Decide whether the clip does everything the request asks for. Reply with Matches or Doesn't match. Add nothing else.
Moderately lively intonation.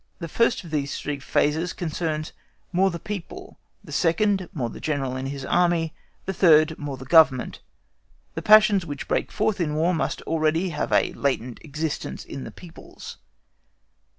Matches